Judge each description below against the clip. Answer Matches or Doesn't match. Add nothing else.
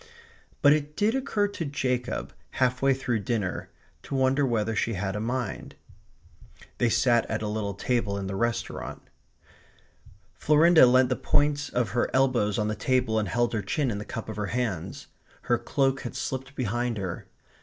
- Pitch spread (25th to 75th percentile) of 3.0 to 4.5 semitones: Matches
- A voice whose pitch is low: Matches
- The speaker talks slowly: Doesn't match